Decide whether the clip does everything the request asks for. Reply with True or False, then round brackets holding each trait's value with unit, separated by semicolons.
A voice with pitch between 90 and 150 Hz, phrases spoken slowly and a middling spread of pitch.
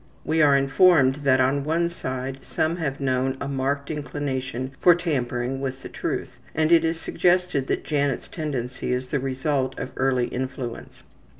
False (135 Hz; 165 wpm; 3.0 semitones)